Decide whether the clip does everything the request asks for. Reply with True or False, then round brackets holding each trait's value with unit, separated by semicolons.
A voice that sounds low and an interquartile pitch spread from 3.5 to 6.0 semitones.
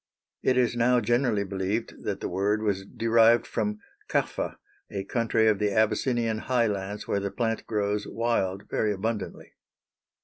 False (110 Hz; 2.5 semitones)